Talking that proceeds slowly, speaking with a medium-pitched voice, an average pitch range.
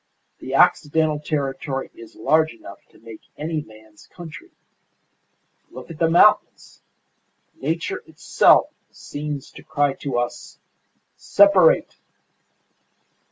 Yes: slow, 105 wpm; medium, 150 Hz; average, 3.6 semitones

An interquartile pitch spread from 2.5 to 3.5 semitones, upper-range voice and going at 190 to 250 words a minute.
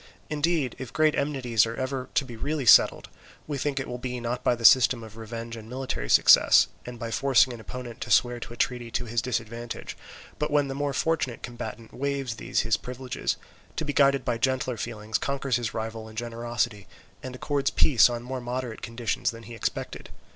No: average, 2.8 semitones; low, 120 Hz; average, 200 wpm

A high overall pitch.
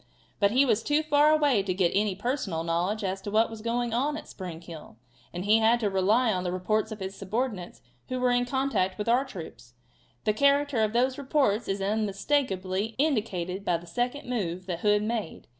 Yes: high, 215 Hz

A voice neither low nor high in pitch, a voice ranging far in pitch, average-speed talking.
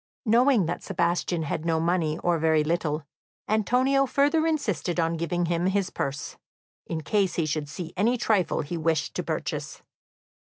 No: medium, 175 Hz; average, 4.8 semitones; average, 160 wpm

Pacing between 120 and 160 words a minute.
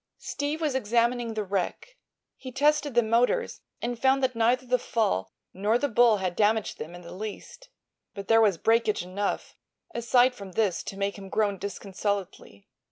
No: average, 170 wpm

